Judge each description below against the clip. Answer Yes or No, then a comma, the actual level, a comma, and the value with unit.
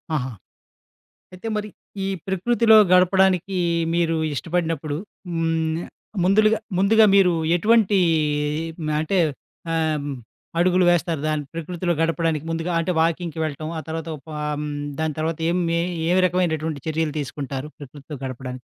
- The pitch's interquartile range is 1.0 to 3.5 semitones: Yes, average, 2.9 semitones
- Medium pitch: Yes, medium, 165 Hz